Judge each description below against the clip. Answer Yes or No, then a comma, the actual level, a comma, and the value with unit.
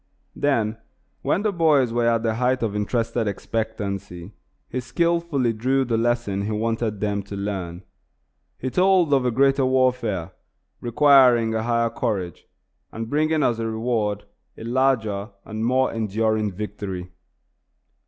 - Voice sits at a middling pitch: No, low, 115 Hz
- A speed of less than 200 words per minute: Yes, average, 140 wpm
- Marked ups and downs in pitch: No, average, 3.6 semitones